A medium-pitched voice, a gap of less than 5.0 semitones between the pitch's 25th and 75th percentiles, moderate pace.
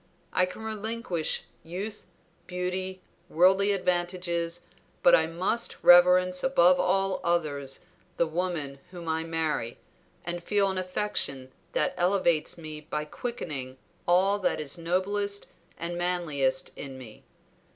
No: medium, 175 Hz; average, 2.9 semitones; slow, 120 wpm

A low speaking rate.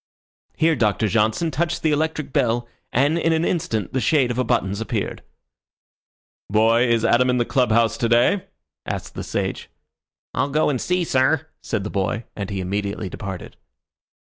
No: average, 170 wpm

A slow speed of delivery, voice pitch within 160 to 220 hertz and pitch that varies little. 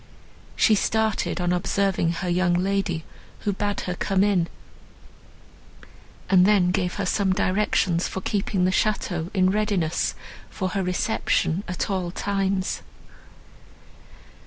Yes: slow, 125 wpm; high, 190 Hz; narrow, 2.0 semitones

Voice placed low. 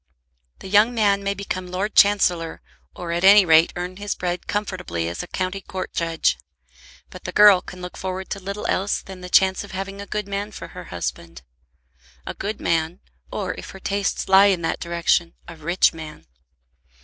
No: medium, 185 Hz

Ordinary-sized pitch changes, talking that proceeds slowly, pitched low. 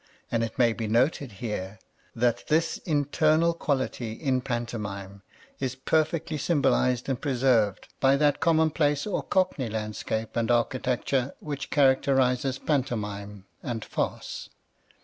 Yes: average, 4.2 semitones; slow, 120 wpm; low, 130 Hz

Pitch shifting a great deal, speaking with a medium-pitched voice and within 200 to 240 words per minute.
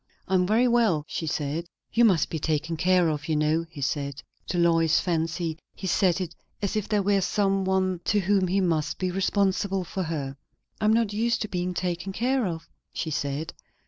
No: average, 3.5 semitones; medium, 180 Hz; fast, 205 wpm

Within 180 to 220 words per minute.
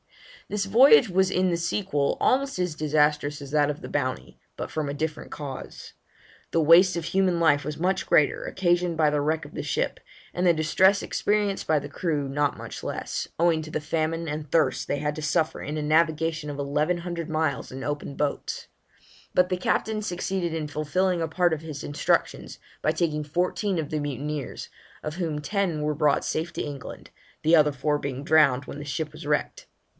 Yes: average, 200 wpm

